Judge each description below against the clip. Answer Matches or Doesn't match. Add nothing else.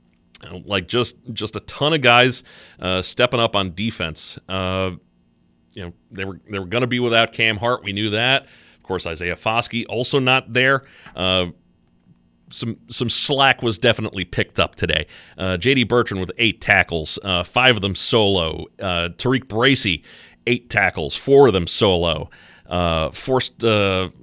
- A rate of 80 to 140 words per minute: Doesn't match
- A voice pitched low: Matches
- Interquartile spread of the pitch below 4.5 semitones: Doesn't match